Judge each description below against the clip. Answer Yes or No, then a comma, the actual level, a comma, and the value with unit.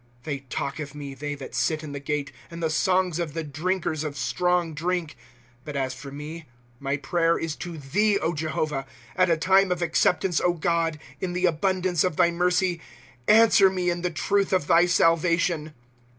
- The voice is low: No, medium, 165 Hz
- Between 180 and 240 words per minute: Yes, average, 195 wpm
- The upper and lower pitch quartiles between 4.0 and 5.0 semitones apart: No, average, 3.2 semitones